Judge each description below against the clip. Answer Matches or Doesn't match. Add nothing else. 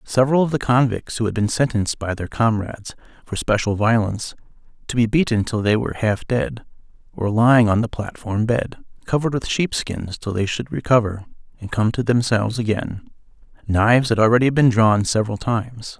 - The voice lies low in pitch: Matches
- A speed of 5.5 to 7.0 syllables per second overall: Matches